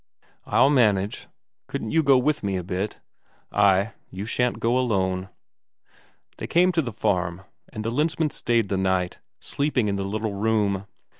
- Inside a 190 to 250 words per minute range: No, average, 160 wpm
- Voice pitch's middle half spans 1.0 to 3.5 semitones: No, average, 4.6 semitones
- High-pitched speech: No, low, 105 Hz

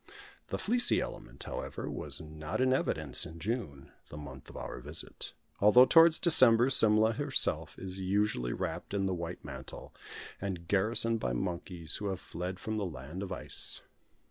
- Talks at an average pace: Yes, average, 165 wpm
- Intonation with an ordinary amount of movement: No, wide, 6.0 semitones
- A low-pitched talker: Yes, very low, 95 Hz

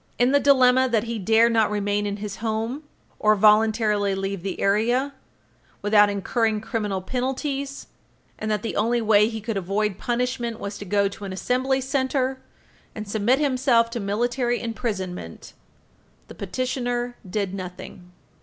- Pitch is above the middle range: Yes, high, 220 Hz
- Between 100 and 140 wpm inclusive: No, average, 150 wpm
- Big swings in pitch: No, average, 3.5 semitones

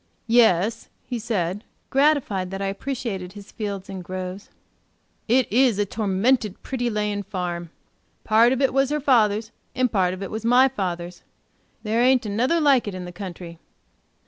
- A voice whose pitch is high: Yes, high, 210 Hz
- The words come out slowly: No, average, 165 wpm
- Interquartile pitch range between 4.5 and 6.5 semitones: Yes, average, 4.8 semitones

